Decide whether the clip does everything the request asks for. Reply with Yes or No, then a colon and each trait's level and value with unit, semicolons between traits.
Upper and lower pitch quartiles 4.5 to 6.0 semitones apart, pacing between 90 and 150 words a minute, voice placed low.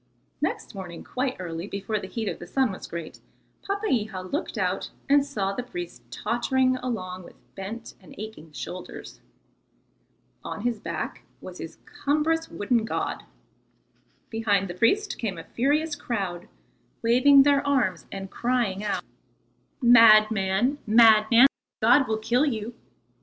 No: average, 4.9 semitones; average, 140 wpm; high, 225 Hz